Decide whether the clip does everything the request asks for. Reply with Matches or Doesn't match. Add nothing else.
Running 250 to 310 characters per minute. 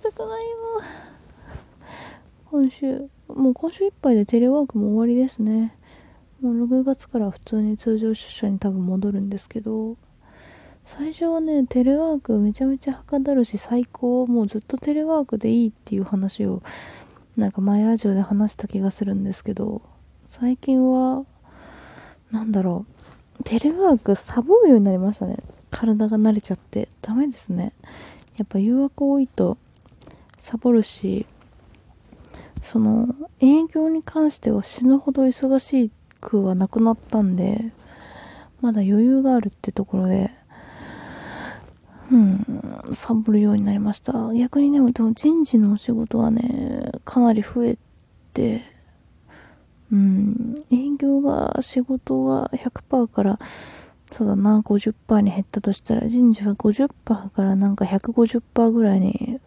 Matches